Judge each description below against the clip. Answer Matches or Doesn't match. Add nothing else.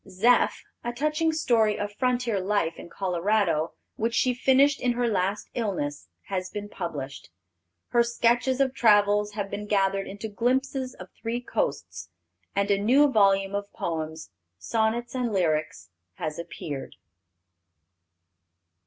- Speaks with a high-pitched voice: Matches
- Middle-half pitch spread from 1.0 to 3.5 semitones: Doesn't match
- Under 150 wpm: Matches